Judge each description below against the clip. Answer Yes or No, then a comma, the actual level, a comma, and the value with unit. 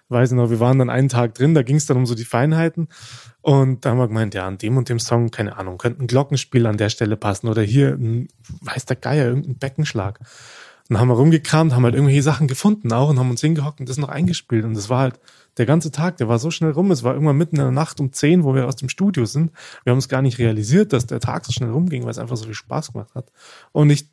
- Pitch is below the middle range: Yes, low, 130 Hz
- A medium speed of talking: No, fast, 280 wpm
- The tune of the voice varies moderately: Yes, average, 3.9 semitones